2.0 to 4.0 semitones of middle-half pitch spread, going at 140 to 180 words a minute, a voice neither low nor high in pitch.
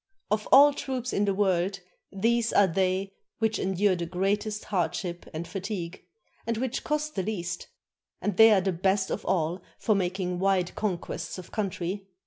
No: average, 2.8 semitones; average, 170 wpm; high, 195 Hz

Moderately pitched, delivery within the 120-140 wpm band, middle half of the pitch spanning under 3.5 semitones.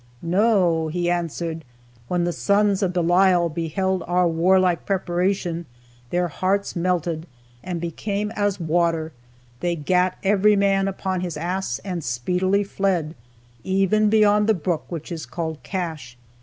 Yes: medium, 180 Hz; slow, 135 wpm; narrow, 2.5 semitones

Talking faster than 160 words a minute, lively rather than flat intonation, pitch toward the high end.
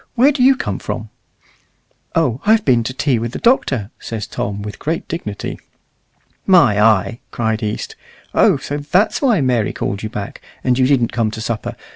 No: average, 180 wpm; wide, 7.1 semitones; low, 125 Hz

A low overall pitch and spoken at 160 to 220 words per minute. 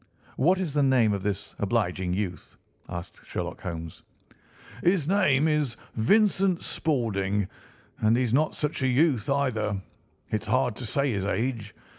No: low, 120 Hz; average, 145 wpm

